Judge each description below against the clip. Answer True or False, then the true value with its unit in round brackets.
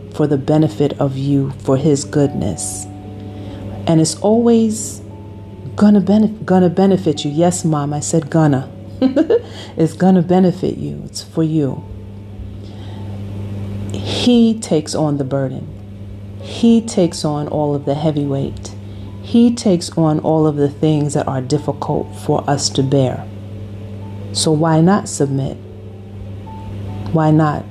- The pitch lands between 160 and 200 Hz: False (140 Hz)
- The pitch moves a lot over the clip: True (7.8 semitones)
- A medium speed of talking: False (130 wpm)